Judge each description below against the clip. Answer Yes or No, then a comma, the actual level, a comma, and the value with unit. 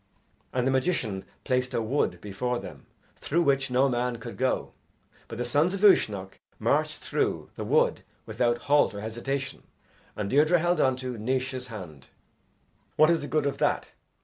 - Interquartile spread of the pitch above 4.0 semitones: No, average, 3.7 semitones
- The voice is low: Yes, low, 125 Hz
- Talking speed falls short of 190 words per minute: Yes, average, 170 wpm